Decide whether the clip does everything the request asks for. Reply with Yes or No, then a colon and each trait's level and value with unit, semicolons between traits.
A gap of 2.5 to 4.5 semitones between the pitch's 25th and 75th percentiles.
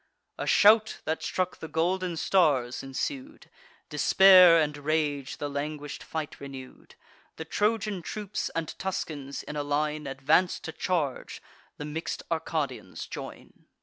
Yes: average, 4.2 semitones